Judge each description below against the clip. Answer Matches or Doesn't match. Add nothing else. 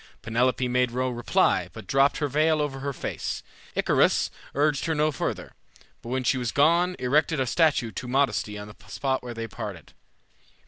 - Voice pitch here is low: Matches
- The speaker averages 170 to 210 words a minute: Matches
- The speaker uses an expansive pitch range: Doesn't match